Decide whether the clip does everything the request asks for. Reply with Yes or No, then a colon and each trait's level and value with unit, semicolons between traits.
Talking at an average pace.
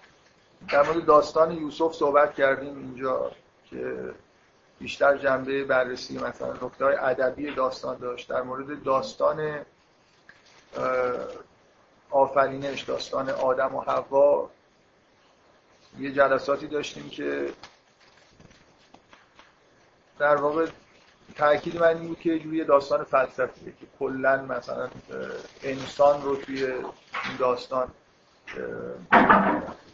No: slow, 90 wpm